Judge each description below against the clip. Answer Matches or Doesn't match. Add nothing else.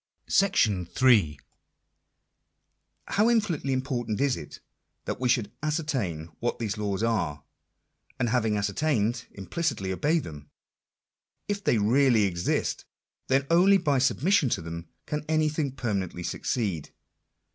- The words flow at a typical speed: Doesn't match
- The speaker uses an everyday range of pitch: Doesn't match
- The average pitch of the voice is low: Matches